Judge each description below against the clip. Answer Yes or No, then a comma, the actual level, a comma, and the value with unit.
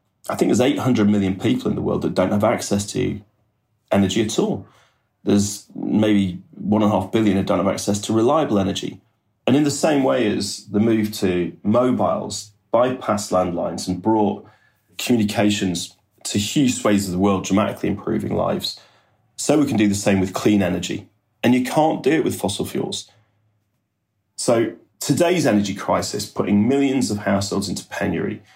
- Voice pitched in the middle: No, low, 105 Hz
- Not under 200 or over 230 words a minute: No, average, 170 wpm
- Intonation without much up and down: Yes, narrow, 1.7 semitones